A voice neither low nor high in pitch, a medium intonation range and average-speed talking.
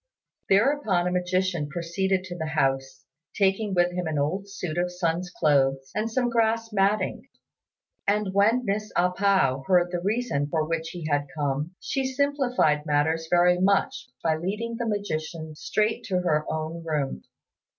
Yes: medium, 180 Hz; average, 4.5 semitones; average, 160 wpm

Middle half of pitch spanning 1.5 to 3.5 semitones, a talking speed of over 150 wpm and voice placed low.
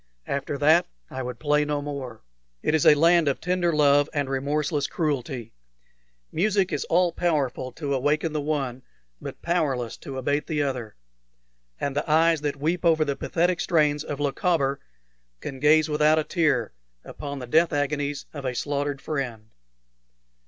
No: narrow, 2.4 semitones; average, 160 wpm; medium, 145 Hz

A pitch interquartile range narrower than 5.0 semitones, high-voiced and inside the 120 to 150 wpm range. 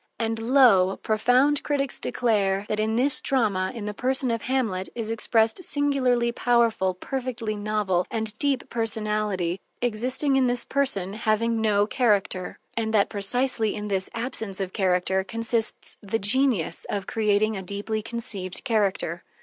Yes: average, 3.4 semitones; high, 220 Hz; average, 145 wpm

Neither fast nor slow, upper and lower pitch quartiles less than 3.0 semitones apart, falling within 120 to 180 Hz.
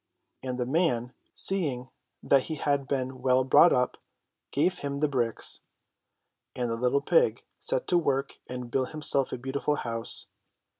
Yes: average, 155 wpm; narrow, 2.6 semitones; low, 135 Hz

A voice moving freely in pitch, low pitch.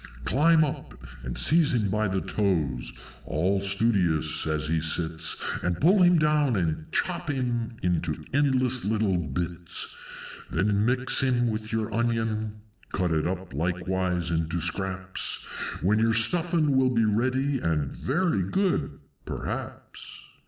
Yes: wide, 6.6 semitones; low, 105 Hz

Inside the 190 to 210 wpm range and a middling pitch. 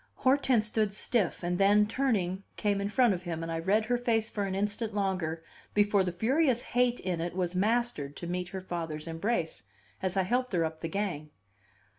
No: average, 200 wpm; high, 195 Hz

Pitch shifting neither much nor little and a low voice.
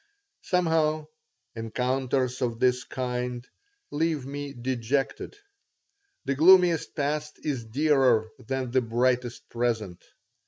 Yes: average, 3.4 semitones; low, 130 Hz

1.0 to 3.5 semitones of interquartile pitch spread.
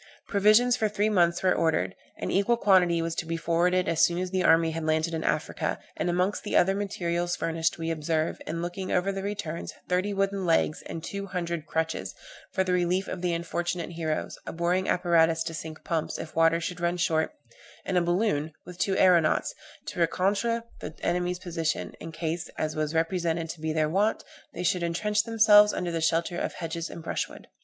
Yes: narrow, 2.4 semitones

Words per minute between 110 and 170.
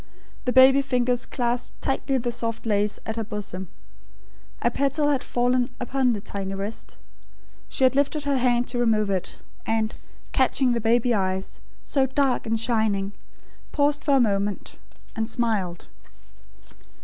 Yes: average, 150 wpm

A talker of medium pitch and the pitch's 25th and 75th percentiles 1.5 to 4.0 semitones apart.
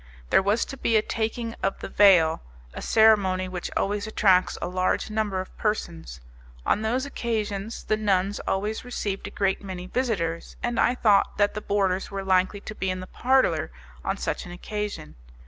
No: high, 205 Hz; average, 2.8 semitones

